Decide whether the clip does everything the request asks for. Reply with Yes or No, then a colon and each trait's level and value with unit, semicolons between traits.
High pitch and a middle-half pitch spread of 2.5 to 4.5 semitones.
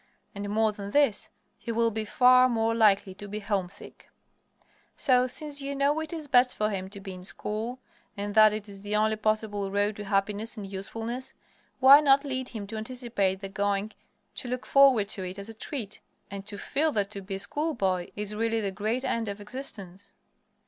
Yes: high, 215 Hz; average, 3.7 semitones